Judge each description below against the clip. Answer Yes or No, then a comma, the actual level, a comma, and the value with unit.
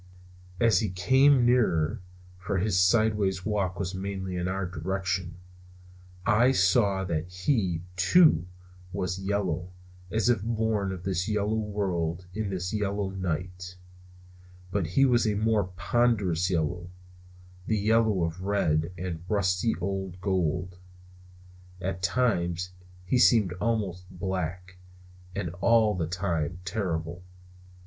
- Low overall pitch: Yes, very low, 95 Hz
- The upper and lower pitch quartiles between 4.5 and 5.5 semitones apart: No, average, 2.9 semitones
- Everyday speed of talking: No, slow, 125 wpm